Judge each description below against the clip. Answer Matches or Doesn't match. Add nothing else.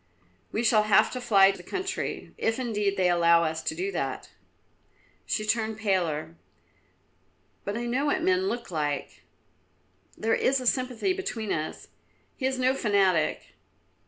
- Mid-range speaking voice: Doesn't match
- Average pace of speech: Matches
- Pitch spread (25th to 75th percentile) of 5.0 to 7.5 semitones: Matches